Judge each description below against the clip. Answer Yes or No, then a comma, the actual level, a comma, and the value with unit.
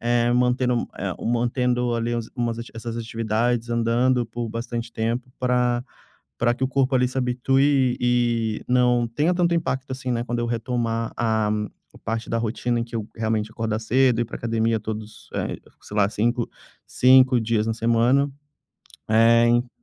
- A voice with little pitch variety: Yes, narrow, 1.5 semitones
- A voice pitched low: Yes, low, 120 Hz